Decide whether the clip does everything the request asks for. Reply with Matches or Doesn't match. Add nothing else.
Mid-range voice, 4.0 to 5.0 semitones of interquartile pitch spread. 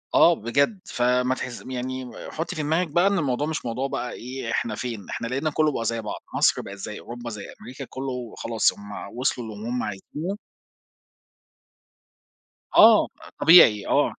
Doesn't match